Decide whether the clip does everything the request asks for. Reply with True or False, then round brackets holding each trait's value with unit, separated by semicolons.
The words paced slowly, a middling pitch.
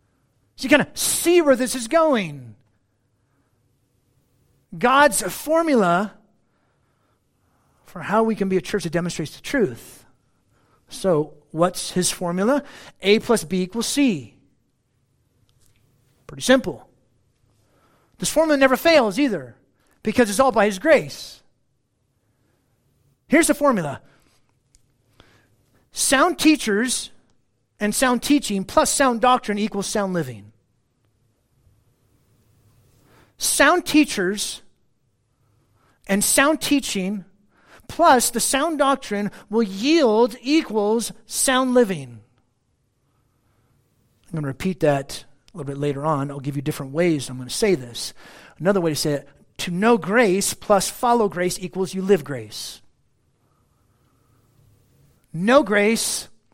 True (115 wpm; 170 Hz)